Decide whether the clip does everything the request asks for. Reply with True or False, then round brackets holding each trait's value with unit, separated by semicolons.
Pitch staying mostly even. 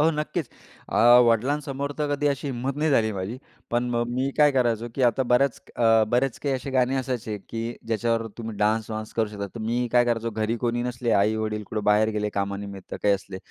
False (3.2 semitones)